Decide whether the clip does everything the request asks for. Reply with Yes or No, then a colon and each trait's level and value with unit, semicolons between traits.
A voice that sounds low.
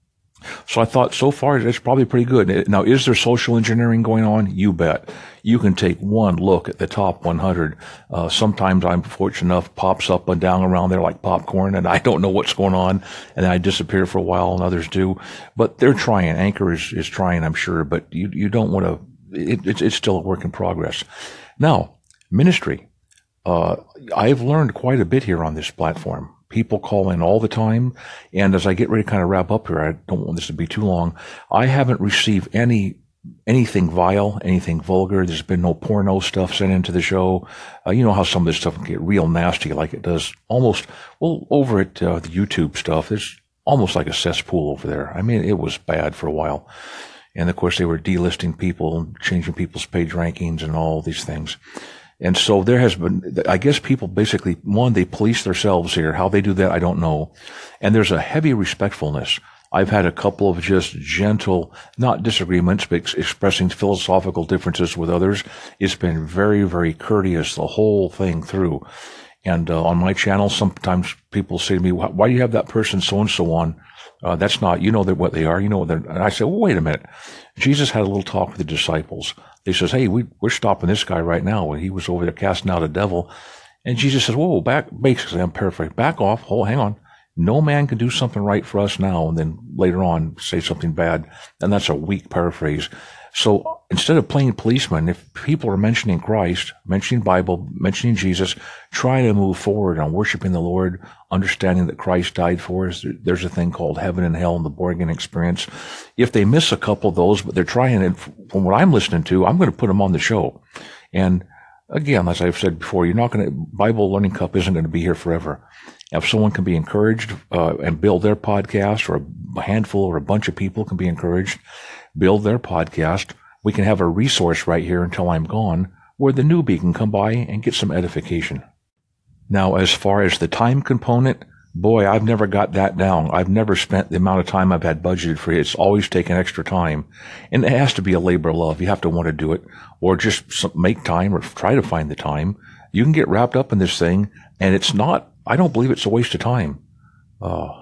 Yes: very low, 95 Hz